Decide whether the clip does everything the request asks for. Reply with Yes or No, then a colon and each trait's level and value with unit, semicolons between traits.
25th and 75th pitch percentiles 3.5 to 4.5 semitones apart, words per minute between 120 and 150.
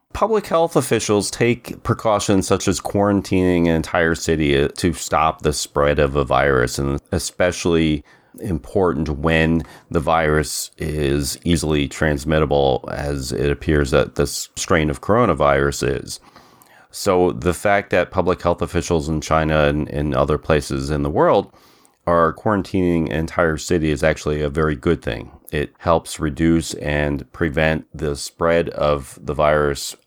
No: average, 2.9 semitones; average, 145 wpm